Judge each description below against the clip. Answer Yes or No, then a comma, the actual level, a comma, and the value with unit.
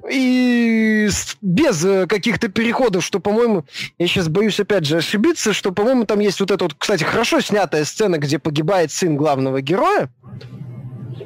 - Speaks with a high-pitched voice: Yes, high, 200 Hz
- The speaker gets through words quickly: No, average, 150 wpm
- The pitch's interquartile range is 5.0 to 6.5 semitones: Yes, wide, 5.4 semitones